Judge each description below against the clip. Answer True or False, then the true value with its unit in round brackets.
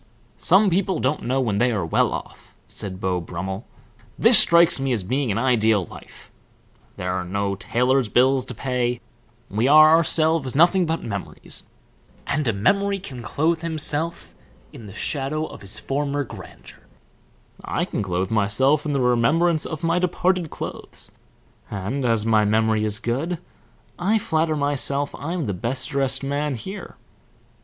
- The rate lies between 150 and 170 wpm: True (155 wpm)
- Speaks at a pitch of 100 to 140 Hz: True (135 Hz)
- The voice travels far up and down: True (6.6 semitones)